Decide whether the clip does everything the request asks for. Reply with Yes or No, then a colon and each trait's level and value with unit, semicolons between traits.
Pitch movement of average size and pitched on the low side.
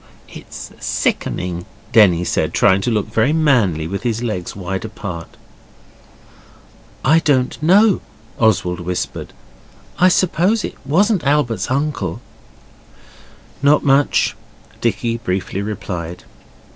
No: wide, 8.0 semitones; low, 115 Hz